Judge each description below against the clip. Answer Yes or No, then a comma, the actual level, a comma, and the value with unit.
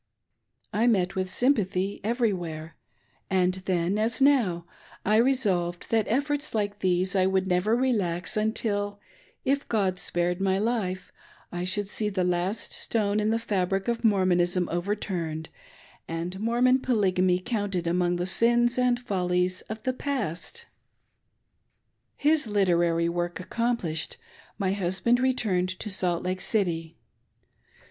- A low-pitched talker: No, high, 195 Hz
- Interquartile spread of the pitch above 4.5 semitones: No, average, 4.2 semitones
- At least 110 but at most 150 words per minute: Yes, slow, 135 wpm